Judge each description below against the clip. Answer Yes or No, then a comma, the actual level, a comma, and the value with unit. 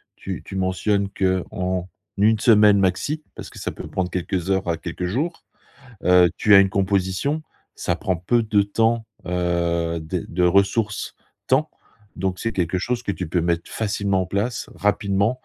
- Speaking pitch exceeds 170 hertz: No, very low, 95 Hz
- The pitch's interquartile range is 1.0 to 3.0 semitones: Yes, average, 2.7 semitones